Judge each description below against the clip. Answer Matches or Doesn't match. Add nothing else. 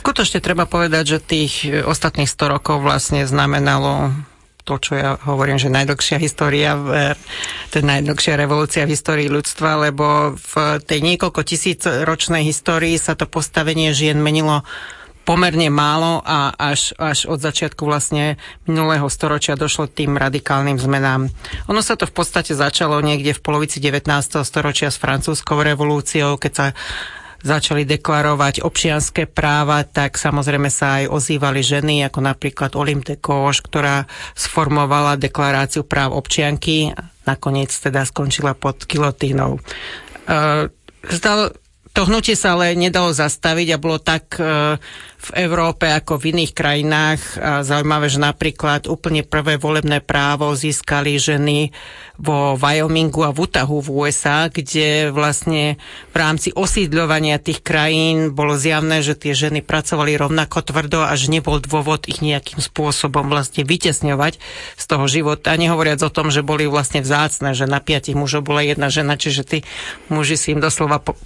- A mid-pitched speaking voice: Matches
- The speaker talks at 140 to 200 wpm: Matches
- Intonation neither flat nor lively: Doesn't match